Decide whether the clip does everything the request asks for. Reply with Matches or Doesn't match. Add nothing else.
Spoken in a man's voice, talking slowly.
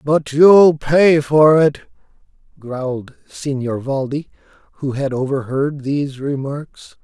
Matches